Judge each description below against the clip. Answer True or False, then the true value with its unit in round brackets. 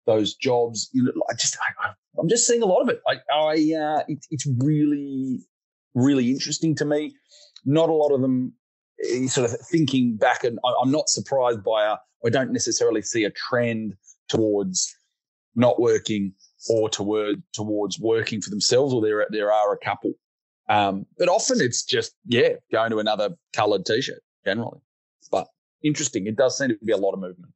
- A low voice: True (130 Hz)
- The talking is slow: False (185 wpm)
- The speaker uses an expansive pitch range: True (6.3 semitones)